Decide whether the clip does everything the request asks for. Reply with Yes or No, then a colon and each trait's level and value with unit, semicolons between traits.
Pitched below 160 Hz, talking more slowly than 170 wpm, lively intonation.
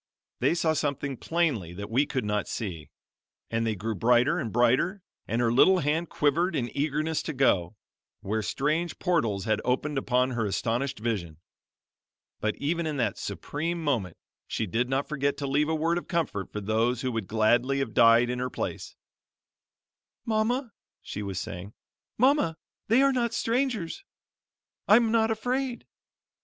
Yes: low, 135 Hz; average, 160 wpm; wide, 6.8 semitones